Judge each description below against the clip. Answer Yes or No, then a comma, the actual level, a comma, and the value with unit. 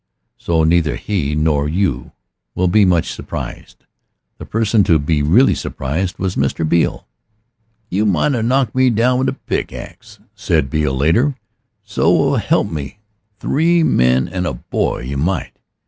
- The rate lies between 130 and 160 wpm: Yes, average, 150 wpm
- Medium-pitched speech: No, very low, 85 Hz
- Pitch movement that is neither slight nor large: No, wide, 6.8 semitones